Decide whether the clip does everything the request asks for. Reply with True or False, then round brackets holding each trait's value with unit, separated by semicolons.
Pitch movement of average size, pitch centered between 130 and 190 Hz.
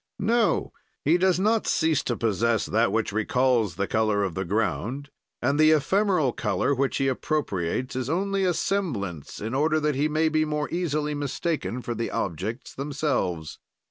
False (5.9 semitones; 140 Hz)